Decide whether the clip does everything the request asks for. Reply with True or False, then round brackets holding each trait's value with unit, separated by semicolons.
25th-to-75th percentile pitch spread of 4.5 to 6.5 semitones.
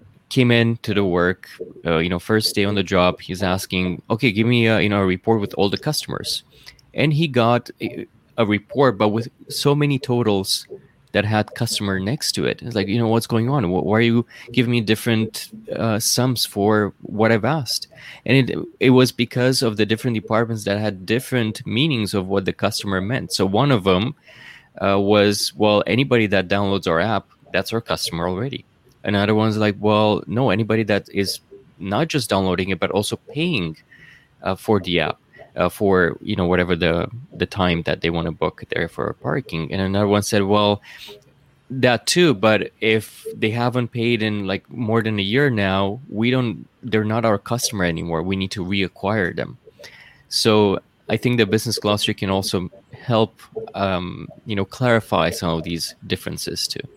False (3.6 semitones)